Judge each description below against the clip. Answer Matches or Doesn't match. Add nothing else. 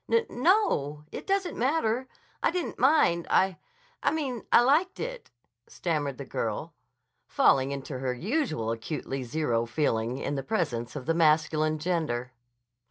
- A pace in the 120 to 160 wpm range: Matches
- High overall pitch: Doesn't match